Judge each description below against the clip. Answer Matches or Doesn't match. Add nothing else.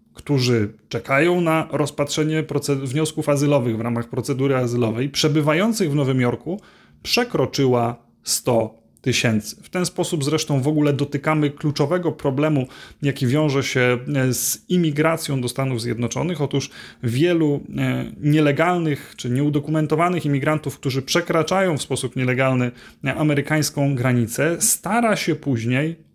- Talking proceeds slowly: Doesn't match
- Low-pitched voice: Doesn't match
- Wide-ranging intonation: Doesn't match